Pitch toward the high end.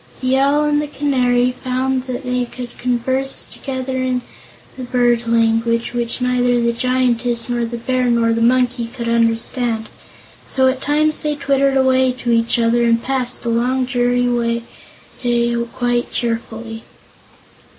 Yes: high, 245 Hz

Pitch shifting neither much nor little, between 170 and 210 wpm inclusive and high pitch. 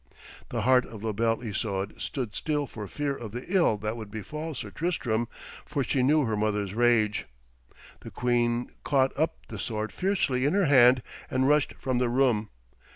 No: average, 4.1 semitones; average, 180 wpm; low, 120 Hz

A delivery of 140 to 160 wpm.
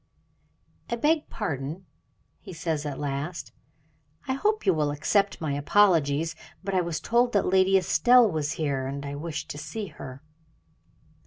Yes: average, 155 wpm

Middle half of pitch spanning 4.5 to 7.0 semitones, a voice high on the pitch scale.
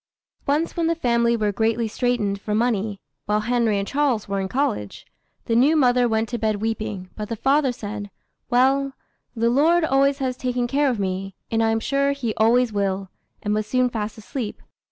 No: average, 3.8 semitones; high, 230 Hz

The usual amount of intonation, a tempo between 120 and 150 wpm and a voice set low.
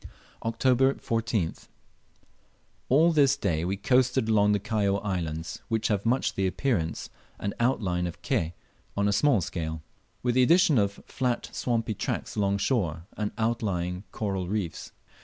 Yes: average, 5.0 semitones; average, 145 wpm; low, 105 Hz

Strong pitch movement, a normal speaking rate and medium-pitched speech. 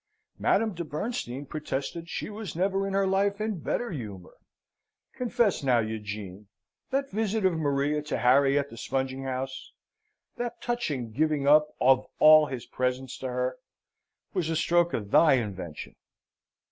Yes: wide, 7.1 semitones; average, 150 wpm; medium, 150 Hz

